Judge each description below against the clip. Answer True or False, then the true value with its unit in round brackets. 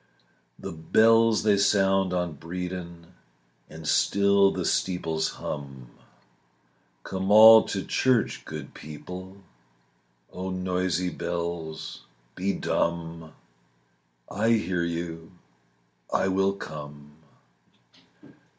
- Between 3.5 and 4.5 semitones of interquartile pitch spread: False (2.9 semitones)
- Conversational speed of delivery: False (90 wpm)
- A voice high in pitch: False (90 Hz)